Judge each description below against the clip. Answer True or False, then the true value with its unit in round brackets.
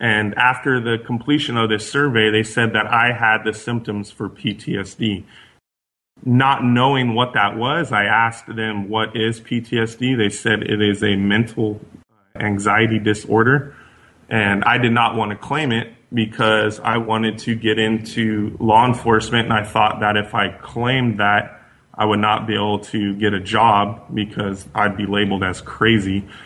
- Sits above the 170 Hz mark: False (110 Hz)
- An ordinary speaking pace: True (170 wpm)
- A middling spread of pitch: False (2.1 semitones)